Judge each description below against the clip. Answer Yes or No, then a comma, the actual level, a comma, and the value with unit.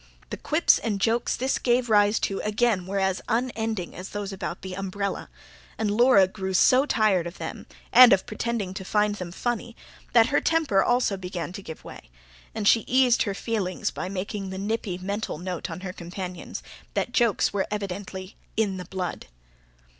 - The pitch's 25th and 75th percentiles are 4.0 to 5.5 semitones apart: No, average, 3.2 semitones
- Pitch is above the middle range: Yes, high, 200 Hz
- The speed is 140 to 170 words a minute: No, average, 180 wpm